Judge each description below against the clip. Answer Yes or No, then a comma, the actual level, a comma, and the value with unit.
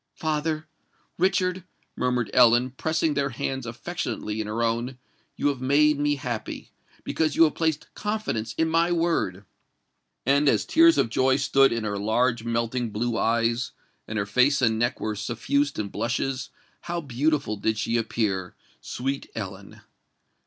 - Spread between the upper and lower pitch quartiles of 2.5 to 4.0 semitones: No, average, 4.8 semitones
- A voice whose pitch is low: Yes, low, 125 Hz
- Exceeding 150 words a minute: No, average, 145 wpm